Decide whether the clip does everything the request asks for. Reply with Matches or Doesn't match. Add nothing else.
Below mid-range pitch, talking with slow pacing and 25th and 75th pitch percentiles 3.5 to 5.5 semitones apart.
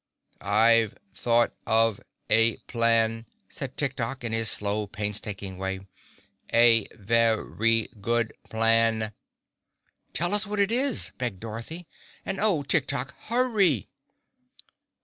Matches